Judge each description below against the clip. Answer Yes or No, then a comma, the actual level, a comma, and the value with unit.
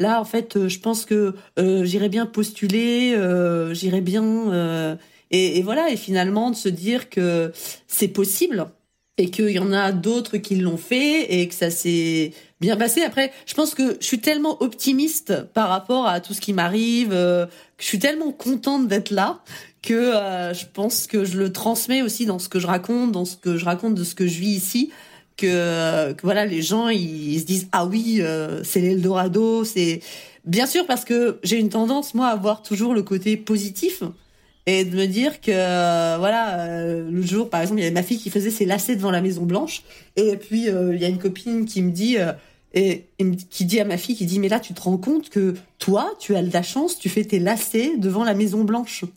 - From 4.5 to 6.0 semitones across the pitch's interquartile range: No, average, 4.0 semitones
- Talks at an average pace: No, fast, 225 wpm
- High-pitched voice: Yes, high, 200 Hz